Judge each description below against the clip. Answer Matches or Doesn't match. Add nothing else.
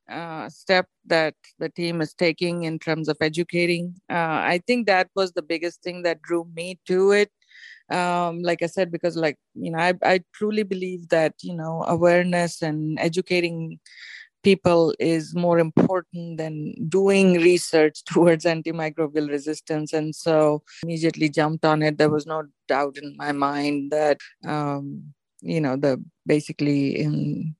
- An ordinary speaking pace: Matches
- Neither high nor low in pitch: Matches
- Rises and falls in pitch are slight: Matches